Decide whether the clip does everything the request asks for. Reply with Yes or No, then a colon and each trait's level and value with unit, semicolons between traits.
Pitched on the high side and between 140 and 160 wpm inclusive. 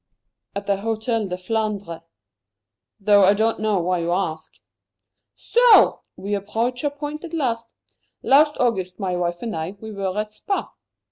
Yes: high, 210 Hz; average, 155 wpm